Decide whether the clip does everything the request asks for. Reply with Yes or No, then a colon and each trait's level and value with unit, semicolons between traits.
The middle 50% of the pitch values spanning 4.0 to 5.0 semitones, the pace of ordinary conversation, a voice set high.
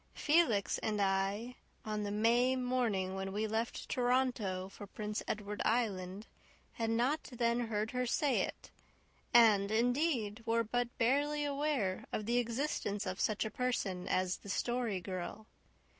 No: average, 3.5 semitones; average, 145 wpm; high, 225 Hz